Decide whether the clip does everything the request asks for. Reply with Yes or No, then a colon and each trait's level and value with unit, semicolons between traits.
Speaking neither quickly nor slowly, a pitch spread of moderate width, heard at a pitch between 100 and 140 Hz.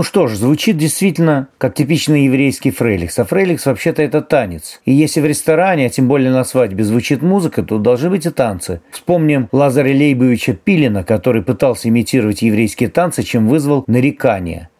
No: fast, 170 wpm; average, 4.5 semitones; low, 135 Hz